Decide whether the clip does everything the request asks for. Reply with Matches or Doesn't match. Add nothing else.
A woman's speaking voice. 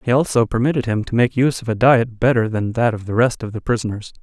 Doesn't match